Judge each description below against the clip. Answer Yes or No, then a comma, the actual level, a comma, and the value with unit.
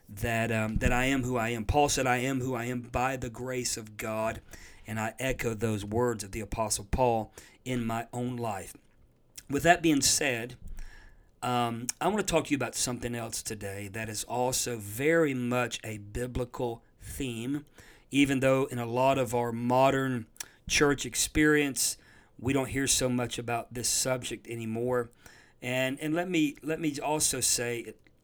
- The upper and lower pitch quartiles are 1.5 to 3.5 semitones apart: Yes, average, 2.7 semitones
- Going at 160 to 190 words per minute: Yes, average, 175 wpm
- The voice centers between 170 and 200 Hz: No, low, 125 Hz